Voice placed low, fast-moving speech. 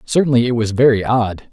No: low, 120 Hz; average, 195 wpm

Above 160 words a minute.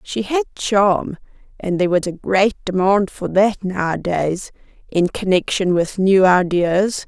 No: average, 145 wpm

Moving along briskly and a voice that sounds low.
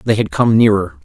Yes: fast, 230 wpm; low, 110 Hz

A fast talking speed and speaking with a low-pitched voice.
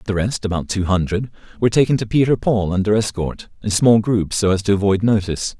Yes: fast, 215 wpm; low, 105 Hz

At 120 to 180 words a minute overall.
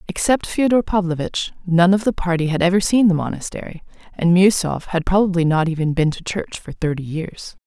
No: average, 190 wpm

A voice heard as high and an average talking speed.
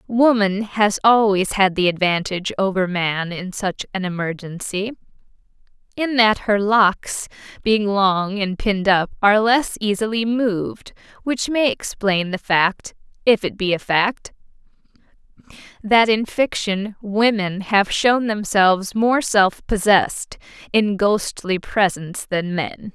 No: high, 205 Hz; slow, 125 wpm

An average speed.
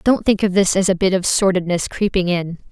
No: fast, 245 wpm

